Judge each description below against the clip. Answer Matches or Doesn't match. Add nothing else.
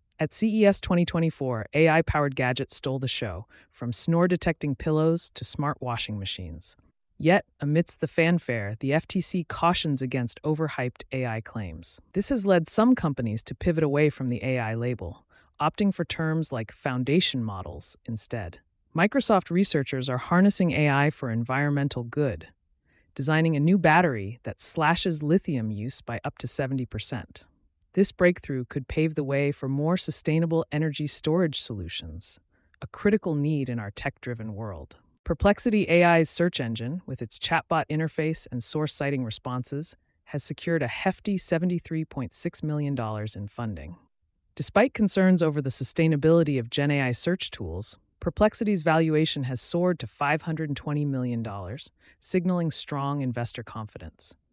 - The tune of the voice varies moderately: Doesn't match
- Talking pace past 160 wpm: Doesn't match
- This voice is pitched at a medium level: Matches